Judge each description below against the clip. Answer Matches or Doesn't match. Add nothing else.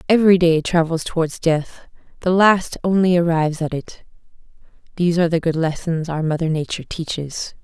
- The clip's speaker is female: Matches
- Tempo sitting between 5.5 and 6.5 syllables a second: Matches